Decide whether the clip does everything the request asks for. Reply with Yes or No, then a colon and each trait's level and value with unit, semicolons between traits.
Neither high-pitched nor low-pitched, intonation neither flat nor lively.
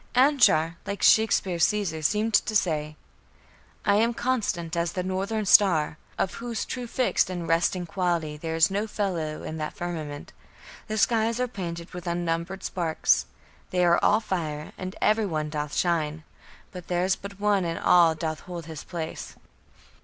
Yes: medium, 175 Hz; average, 4.1 semitones